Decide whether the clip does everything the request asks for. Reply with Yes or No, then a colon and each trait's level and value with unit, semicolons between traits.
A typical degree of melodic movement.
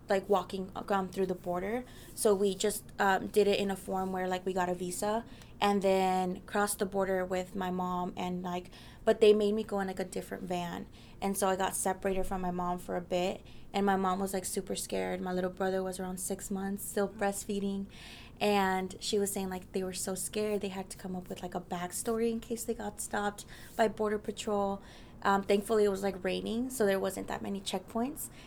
No: narrow, 1.8 semitones